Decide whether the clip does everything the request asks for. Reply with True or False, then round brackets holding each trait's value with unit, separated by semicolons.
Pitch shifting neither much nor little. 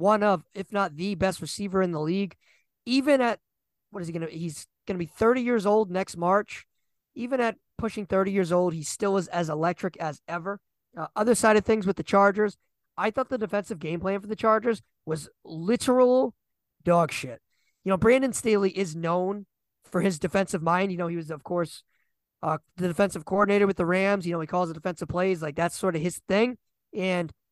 True (3.6 semitones)